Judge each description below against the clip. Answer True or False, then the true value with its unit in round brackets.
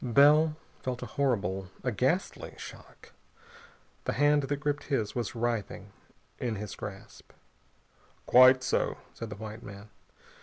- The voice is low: True (125 Hz)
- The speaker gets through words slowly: True (130 wpm)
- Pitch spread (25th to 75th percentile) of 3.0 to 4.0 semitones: False (5.0 semitones)